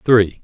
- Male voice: Yes, male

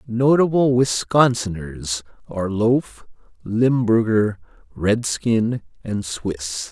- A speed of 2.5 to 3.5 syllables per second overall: Yes, 3.2 syllables/s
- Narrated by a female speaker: No, male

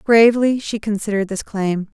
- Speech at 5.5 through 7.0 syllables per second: No, 5.3 syllables/s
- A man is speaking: No, female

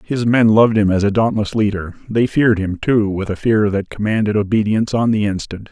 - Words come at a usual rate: No, fast, 220 wpm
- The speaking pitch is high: No, low, 105 Hz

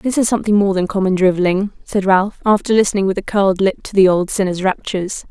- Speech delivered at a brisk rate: Yes, fast, 225 wpm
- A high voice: Yes, high, 195 Hz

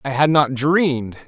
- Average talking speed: Yes, average, 190 wpm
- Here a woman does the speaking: No, male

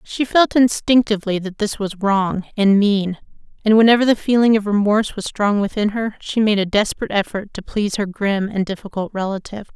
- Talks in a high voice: Yes, high, 210 Hz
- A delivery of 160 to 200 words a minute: Yes, average, 190 wpm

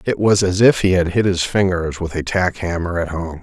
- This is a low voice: Yes, very low, 90 Hz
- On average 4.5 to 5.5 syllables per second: Yes, 5.1 syllables/s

